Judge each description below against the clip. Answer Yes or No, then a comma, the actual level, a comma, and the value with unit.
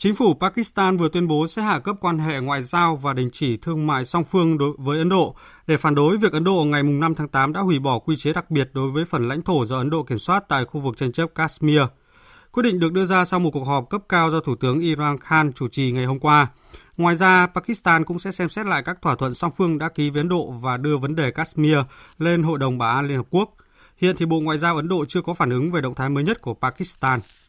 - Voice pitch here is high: No, medium, 160 Hz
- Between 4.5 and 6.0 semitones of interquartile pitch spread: No, average, 4.0 semitones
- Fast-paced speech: Yes, fast, 275 wpm